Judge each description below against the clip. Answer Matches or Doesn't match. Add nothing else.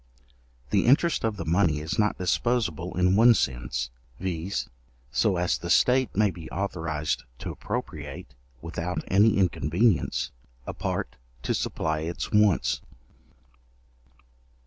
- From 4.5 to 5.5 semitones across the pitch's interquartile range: Matches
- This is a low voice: Matches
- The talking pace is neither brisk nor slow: Doesn't match